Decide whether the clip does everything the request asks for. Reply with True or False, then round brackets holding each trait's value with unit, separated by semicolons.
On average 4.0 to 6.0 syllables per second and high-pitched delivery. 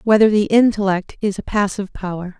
True (5.8 syllables/s; 200 Hz)